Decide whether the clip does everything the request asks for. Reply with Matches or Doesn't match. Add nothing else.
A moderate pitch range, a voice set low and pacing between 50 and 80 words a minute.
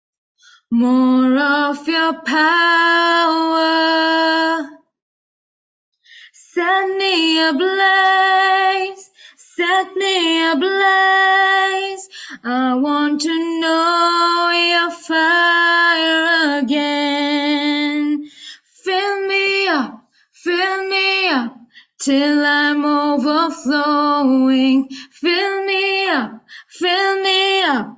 Doesn't match